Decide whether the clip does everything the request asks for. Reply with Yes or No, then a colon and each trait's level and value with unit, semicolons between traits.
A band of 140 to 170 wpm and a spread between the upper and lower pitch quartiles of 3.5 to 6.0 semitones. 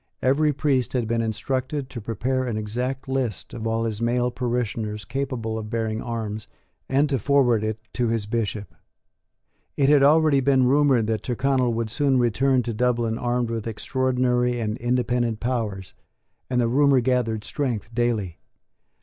No: average, 160 wpm; average, 2.7 semitones